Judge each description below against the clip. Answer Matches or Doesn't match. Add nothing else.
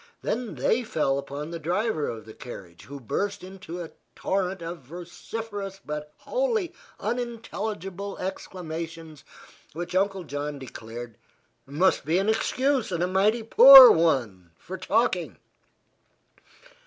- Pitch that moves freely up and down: Matches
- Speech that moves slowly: Matches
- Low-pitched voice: Doesn't match